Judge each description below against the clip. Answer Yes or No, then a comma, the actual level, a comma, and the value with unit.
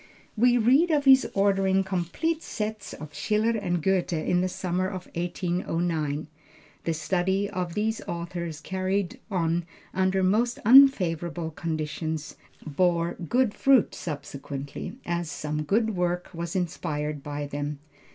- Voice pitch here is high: No, medium, 175 Hz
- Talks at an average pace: No, slow, 130 wpm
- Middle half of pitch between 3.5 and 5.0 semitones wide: Yes, average, 3.9 semitones